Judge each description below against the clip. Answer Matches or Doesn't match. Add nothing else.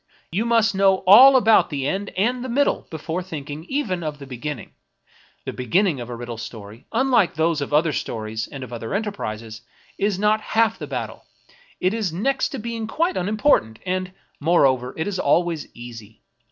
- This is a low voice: Doesn't match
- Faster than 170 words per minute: Matches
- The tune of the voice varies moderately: Doesn't match